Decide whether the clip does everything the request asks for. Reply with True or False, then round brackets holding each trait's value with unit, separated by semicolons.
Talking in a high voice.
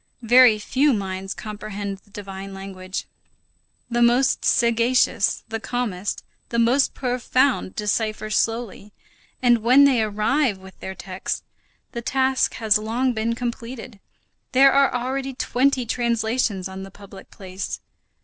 True (230 Hz)